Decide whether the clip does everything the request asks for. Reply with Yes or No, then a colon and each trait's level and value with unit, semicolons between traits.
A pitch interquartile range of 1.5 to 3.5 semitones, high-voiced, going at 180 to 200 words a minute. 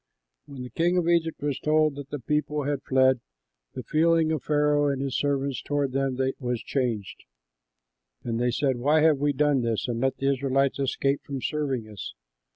No: narrow, 2.4 semitones; medium, 140 Hz; average, 185 wpm